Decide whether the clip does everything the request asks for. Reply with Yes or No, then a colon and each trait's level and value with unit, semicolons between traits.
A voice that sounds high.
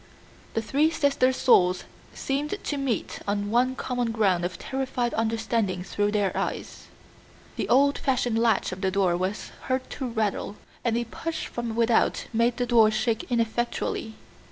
Yes: high, 230 Hz